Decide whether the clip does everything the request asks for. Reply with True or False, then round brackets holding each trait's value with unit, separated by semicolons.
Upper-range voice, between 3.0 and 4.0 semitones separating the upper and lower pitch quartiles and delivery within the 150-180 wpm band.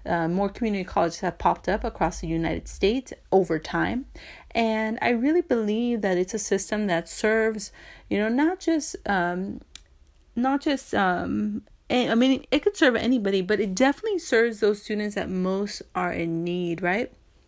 False (215 Hz; 5.1 semitones; 170 wpm)